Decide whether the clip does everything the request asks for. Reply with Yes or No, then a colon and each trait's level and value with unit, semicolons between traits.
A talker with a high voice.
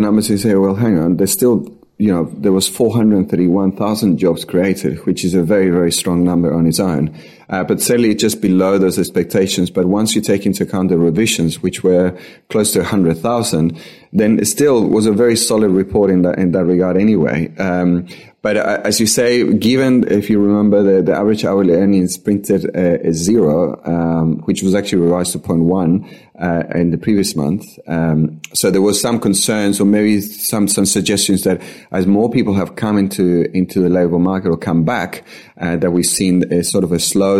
No: very low, 95 Hz